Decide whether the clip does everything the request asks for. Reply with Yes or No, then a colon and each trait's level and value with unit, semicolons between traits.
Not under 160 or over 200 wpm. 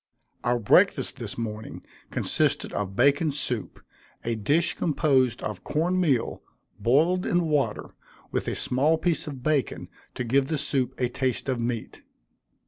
No: average, 145 wpm